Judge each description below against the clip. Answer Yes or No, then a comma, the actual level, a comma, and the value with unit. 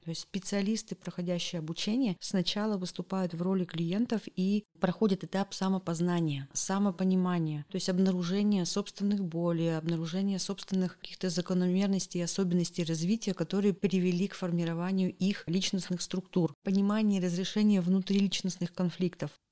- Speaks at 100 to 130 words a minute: Yes, average, 120 wpm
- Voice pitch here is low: No, medium, 185 Hz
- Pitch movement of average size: No, narrow, 2.0 semitones